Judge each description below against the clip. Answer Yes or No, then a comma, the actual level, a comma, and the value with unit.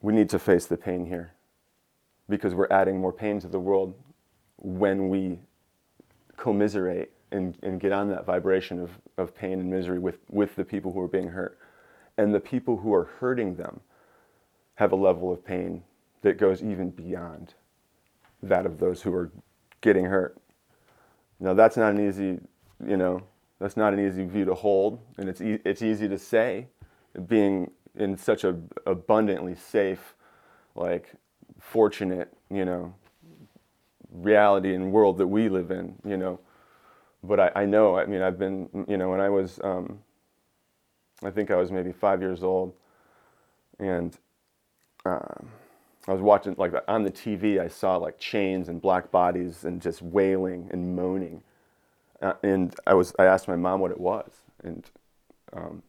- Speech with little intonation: Yes, narrow, 1.9 semitones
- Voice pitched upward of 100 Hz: No, very low, 95 Hz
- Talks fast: No, average, 170 wpm